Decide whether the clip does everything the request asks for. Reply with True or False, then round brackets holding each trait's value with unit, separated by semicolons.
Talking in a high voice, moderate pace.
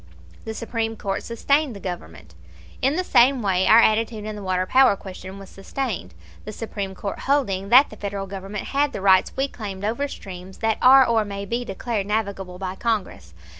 True (210 Hz; 190 wpm)